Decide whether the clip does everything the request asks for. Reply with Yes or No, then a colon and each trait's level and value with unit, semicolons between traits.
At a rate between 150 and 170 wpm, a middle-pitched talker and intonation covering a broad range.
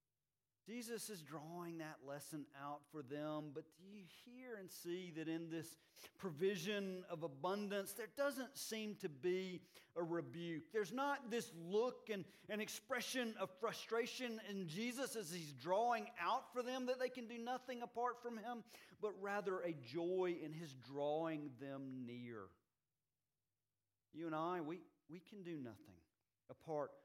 Yes: average, 155 wpm; medium, 180 Hz; wide, 6.6 semitones